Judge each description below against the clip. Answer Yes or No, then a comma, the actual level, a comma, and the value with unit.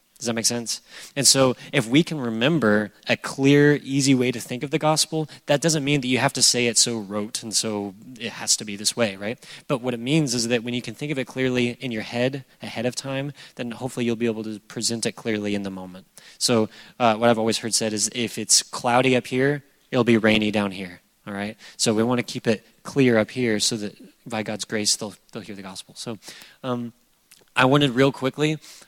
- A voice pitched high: No, low, 120 Hz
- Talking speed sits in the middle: No, fast, 240 wpm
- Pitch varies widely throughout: No, average, 3.7 semitones